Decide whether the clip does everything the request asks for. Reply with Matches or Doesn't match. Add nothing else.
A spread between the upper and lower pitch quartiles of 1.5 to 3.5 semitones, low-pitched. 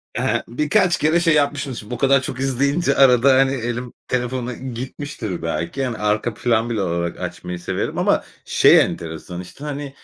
Doesn't match